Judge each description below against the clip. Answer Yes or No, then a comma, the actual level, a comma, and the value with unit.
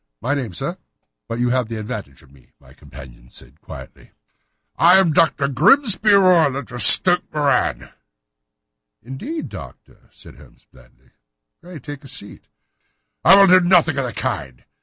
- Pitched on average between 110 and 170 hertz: Yes, medium, 140 Hz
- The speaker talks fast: No, average, 155 wpm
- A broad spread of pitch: Yes, wide, 7.7 semitones